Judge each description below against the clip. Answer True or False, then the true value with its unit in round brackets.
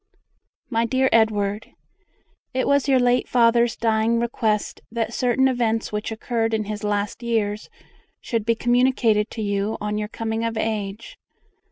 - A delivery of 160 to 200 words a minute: False (150 wpm)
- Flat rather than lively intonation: True (2.0 semitones)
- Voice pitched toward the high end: True (225 Hz)